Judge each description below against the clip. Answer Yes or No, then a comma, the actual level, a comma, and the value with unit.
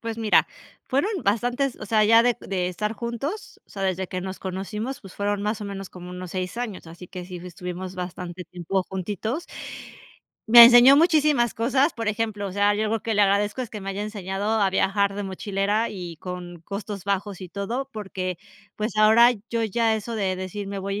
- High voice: Yes, high, 205 Hz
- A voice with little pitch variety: No, average, 3.3 semitones